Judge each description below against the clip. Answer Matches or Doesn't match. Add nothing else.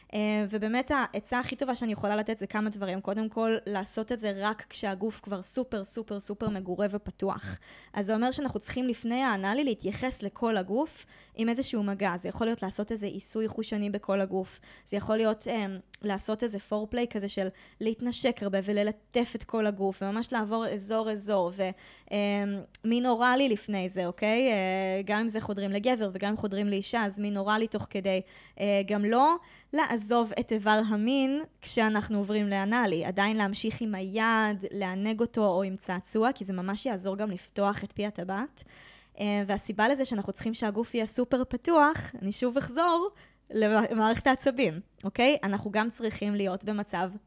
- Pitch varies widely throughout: Doesn't match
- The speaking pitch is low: Doesn't match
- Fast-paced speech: Matches